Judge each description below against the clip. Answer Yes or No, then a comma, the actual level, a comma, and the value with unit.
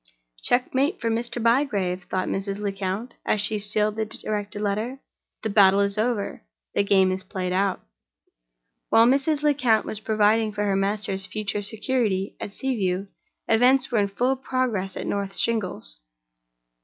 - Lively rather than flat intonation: No, average, 3.1 semitones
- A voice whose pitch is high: Yes, high, 210 Hz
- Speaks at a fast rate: No, average, 155 wpm